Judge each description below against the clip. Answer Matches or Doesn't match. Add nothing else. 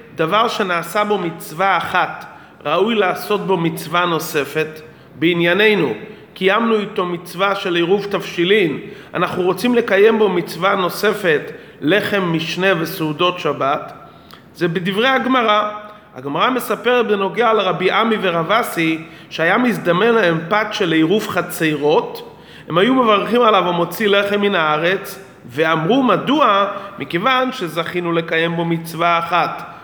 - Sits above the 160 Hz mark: Matches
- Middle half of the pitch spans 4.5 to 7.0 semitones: Doesn't match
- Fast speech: Doesn't match